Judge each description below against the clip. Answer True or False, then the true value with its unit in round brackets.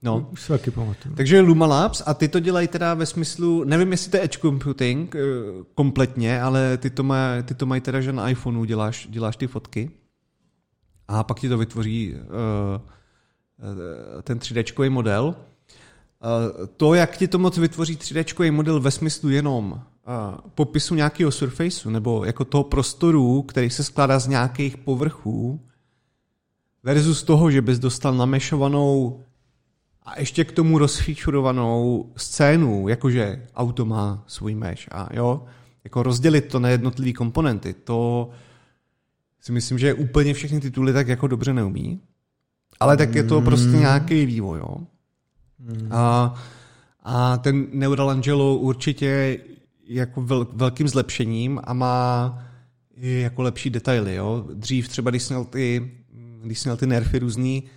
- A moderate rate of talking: True (140 wpm)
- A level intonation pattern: False (3.0 semitones)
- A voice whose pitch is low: True (130 Hz)